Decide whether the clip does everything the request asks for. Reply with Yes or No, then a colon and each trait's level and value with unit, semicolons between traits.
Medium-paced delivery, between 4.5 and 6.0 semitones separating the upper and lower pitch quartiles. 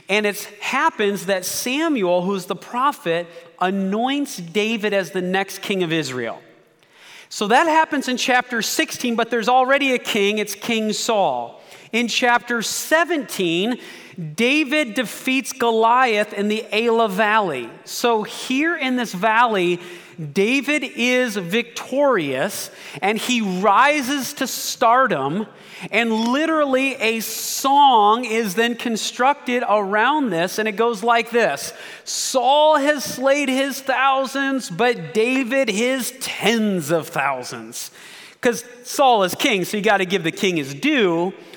No: slow, 130 wpm; average, 4.8 semitones